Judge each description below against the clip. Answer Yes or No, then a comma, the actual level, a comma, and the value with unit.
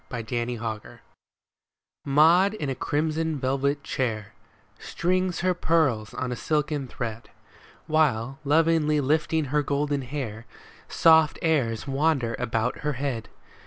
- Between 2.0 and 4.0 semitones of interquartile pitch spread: No, average, 4.5 semitones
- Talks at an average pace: No, slow, 125 wpm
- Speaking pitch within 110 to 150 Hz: Yes, medium, 140 Hz